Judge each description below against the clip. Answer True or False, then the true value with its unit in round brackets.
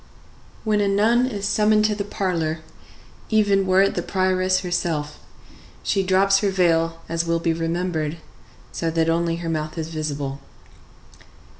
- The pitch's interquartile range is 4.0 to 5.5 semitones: False (3.2 semitones)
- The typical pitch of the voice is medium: True (180 Hz)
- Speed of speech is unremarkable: True (150 wpm)